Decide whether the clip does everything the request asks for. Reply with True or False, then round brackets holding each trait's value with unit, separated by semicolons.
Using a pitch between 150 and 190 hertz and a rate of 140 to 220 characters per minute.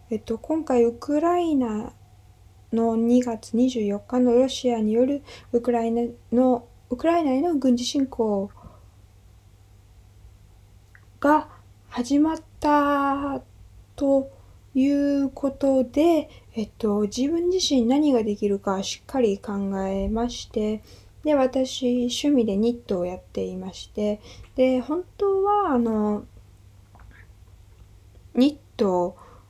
False (230 Hz; 195 characters per minute)